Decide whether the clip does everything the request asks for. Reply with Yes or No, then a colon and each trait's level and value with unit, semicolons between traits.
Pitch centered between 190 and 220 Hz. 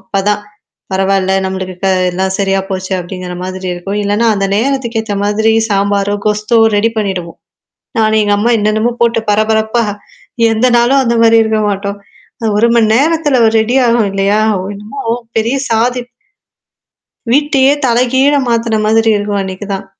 Yes: high, 215 Hz